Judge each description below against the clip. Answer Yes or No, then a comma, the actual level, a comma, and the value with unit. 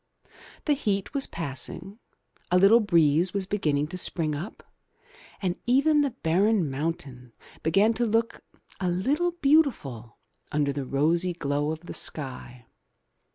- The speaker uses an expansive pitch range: Yes, wide, 7.1 semitones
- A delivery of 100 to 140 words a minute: Yes, slow, 135 wpm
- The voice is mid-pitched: Yes, medium, 175 Hz